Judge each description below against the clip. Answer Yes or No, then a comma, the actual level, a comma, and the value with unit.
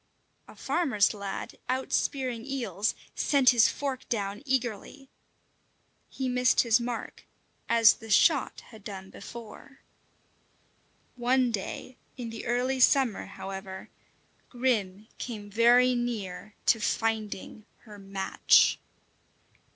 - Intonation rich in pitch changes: No, average, 3.6 semitones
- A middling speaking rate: No, slow, 110 wpm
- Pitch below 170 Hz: No, high, 230 Hz